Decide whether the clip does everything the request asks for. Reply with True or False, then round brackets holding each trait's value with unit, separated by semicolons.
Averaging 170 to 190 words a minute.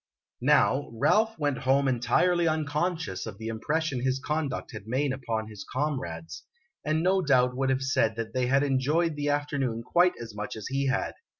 True (180 wpm)